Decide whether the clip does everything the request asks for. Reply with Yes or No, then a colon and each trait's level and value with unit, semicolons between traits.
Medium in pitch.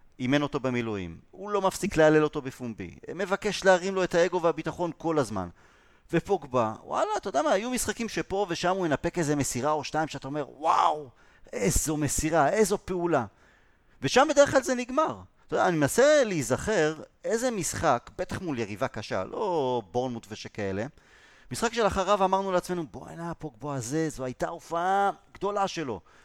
Yes: medium, 160 Hz